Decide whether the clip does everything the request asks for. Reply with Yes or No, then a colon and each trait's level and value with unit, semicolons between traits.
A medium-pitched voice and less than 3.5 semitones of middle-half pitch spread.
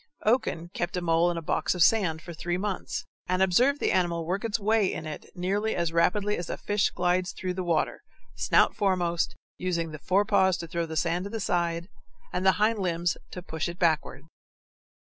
Yes: medium, 180 Hz; average, 2.8 semitones